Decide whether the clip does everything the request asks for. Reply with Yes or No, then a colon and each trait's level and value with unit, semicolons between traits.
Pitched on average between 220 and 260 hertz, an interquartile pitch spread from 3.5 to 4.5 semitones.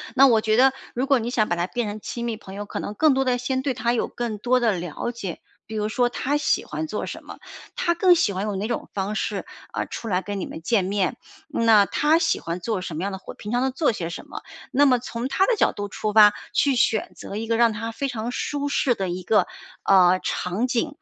Yes: high, 225 Hz; average, 4.1 semitones